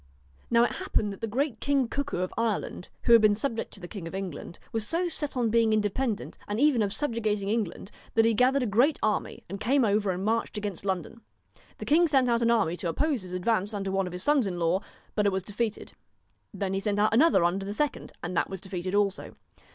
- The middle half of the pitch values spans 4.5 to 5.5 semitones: No, average, 3.6 semitones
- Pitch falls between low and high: No, high, 215 Hz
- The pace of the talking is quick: Yes, fast, 230 wpm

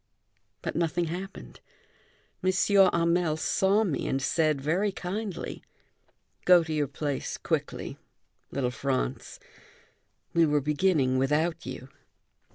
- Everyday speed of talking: No, slow, 110 wpm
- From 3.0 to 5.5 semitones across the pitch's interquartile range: Yes, average, 4.3 semitones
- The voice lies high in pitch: No, medium, 165 Hz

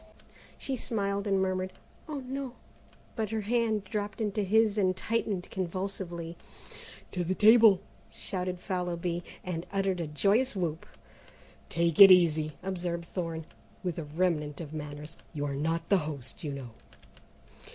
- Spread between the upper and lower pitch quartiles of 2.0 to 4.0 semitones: Yes, average, 3.5 semitones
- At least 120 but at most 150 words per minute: Yes, average, 140 wpm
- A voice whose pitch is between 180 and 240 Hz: Yes, medium, 185 Hz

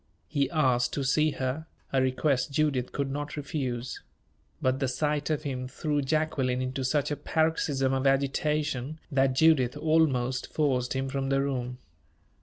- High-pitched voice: No, low, 135 Hz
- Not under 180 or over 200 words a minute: No, average, 155 wpm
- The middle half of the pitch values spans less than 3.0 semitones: Yes, narrow, 2.6 semitones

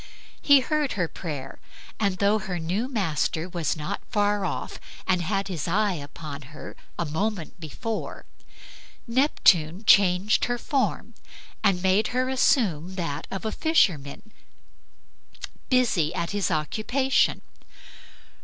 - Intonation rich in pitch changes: No, average, 5.0 semitones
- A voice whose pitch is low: No, high, 190 Hz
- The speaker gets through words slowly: Yes, slow, 125 wpm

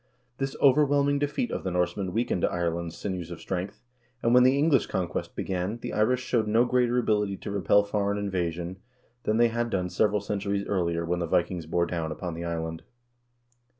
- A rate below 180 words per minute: No, average, 185 wpm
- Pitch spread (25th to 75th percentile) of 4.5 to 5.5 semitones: Yes, average, 5.2 semitones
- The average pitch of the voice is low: Yes, low, 100 Hz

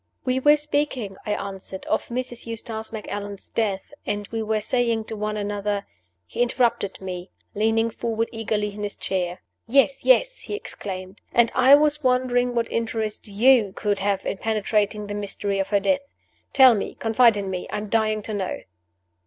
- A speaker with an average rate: Yes, average, 180 wpm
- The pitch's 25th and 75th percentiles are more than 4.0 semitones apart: No, average, 3.1 semitones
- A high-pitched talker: Yes, high, 220 Hz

